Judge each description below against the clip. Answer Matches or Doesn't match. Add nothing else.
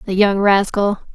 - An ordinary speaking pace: Matches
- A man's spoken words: Doesn't match